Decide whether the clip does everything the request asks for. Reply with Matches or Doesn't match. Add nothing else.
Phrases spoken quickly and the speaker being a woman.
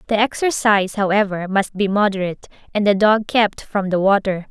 Doesn't match